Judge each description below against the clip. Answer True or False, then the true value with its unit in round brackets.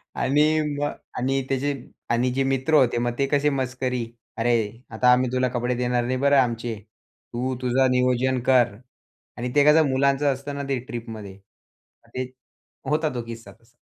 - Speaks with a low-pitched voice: True (130 Hz)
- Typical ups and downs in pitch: False (2.2 semitones)